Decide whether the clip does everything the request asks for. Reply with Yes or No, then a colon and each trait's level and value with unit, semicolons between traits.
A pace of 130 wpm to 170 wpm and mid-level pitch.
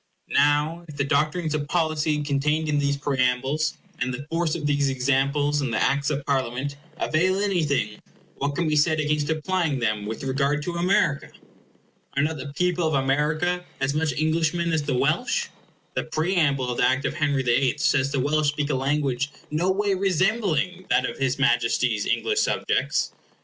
No: average, 180 wpm; medium, 145 Hz